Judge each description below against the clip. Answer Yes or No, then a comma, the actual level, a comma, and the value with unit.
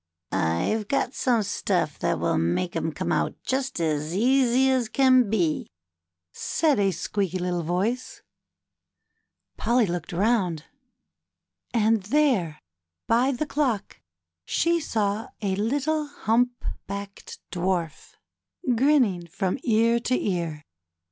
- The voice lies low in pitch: No, high, 215 Hz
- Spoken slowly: Yes, slow, 115 wpm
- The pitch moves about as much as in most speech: No, wide, 6.1 semitones